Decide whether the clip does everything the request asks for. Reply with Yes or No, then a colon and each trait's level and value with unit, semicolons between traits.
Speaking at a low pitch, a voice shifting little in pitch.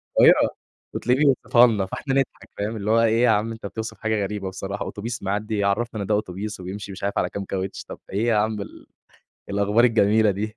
Yes: low, 105 Hz; narrow, 2.2 semitones